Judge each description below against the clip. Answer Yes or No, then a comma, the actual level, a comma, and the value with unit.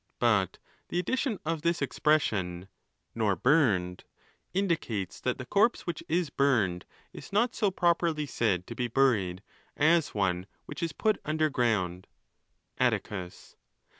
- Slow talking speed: Yes, slow, 130 wpm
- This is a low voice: Yes, low, 130 Hz